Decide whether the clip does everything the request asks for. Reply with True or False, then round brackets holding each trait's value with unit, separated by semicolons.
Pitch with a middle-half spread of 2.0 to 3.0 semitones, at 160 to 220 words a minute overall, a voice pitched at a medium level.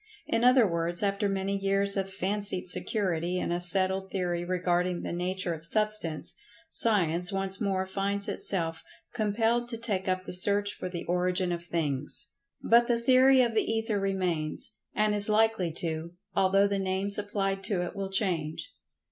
False (2.7 semitones; 165 wpm; 195 Hz)